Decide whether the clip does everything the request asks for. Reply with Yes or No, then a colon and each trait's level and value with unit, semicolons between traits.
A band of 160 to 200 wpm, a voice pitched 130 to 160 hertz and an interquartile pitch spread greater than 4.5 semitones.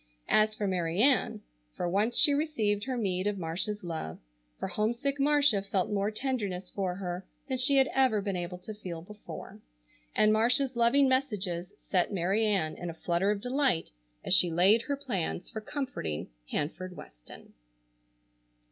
No: average, 165 wpm; high, 205 Hz; wide, 5.6 semitones